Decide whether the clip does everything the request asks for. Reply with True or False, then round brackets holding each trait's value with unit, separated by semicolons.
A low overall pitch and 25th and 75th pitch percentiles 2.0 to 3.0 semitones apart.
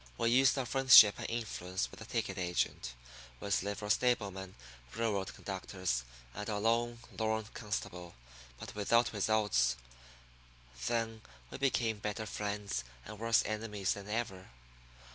True (105 Hz; 2.7 semitones)